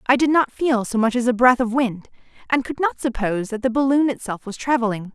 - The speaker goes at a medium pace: No, fast, 245 wpm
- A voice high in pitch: Yes, high, 245 Hz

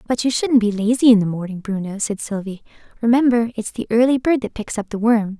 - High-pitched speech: Yes, high, 225 Hz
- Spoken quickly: Yes, fast, 235 wpm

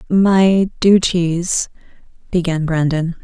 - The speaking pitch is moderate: Yes, medium, 175 Hz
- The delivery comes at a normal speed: No, slow, 75 wpm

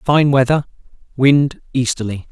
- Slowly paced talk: Yes, slow, 105 wpm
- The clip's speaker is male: Yes, male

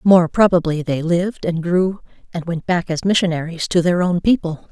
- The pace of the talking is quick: No, average, 190 wpm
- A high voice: No, medium, 175 Hz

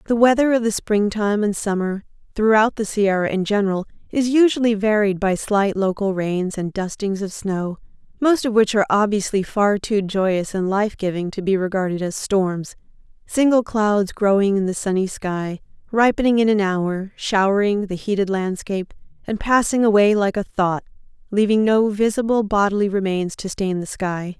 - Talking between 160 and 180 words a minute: Yes, average, 165 wpm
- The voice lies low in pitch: No, high, 205 Hz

